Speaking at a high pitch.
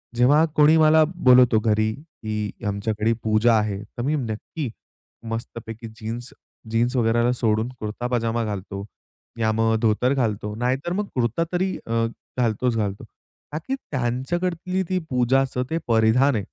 No: low, 120 Hz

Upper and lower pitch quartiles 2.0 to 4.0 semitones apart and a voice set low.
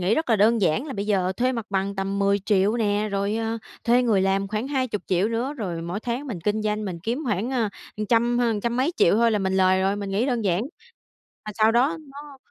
No: average, 3.4 semitones; high, 215 Hz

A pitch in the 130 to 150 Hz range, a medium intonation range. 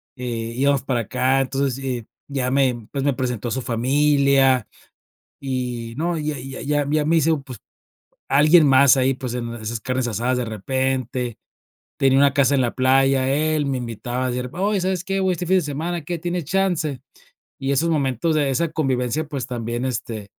Yes: low, 135 Hz; average, 3.1 semitones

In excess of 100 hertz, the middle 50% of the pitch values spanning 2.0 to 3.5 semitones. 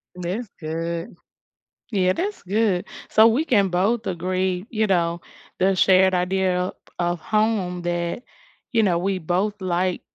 Yes: medium, 185 Hz; average, 2.8 semitones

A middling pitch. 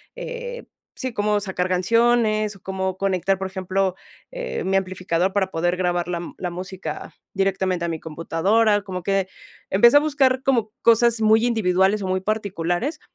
No: high, 195 Hz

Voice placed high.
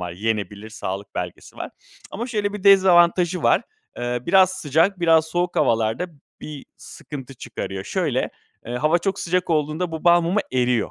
No: medium, 160 Hz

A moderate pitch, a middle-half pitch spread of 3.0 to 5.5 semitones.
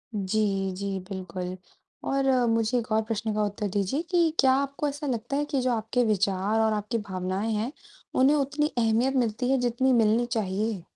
No: high, 225 Hz; average, 4.2 semitones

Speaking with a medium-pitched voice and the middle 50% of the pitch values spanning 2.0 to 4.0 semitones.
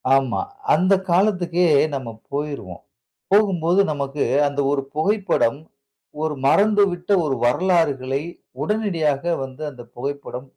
No: medium, 155 Hz; average, 5.2 semitones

